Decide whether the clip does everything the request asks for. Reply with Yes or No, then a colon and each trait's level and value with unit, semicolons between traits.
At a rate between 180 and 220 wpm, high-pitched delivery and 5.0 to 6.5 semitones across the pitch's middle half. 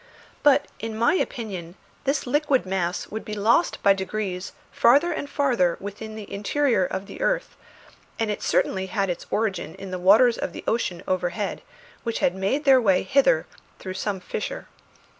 No: average, 170 wpm; high, 210 Hz; wide, 5.4 semitones